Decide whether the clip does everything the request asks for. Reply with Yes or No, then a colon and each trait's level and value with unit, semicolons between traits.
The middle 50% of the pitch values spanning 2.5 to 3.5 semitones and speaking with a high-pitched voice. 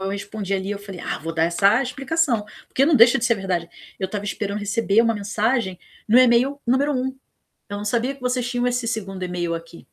No: average, 4.3 semitones; high, 215 Hz